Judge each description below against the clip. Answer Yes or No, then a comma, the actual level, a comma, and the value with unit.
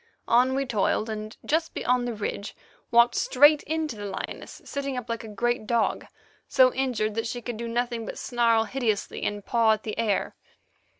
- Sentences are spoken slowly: No, average, 185 wpm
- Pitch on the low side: No, high, 235 Hz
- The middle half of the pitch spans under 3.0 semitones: Yes, narrow, 2.6 semitones